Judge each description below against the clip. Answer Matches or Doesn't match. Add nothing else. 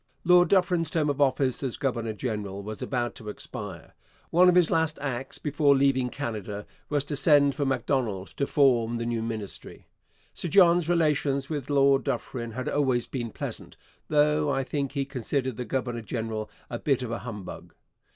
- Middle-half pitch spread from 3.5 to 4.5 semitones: Matches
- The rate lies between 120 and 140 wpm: Doesn't match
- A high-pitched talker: Doesn't match